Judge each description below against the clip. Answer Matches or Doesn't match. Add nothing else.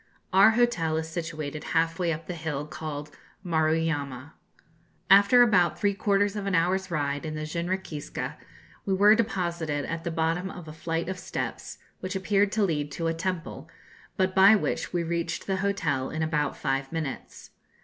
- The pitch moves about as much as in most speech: Matches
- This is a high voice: Doesn't match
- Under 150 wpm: Doesn't match